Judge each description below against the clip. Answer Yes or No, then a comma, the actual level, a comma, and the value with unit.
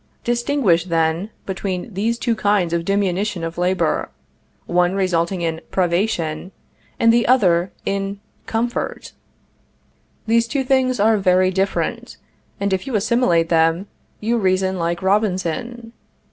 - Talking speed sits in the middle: No, slow, 125 wpm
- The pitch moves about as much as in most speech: Yes, average, 4.4 semitones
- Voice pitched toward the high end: Yes, high, 195 Hz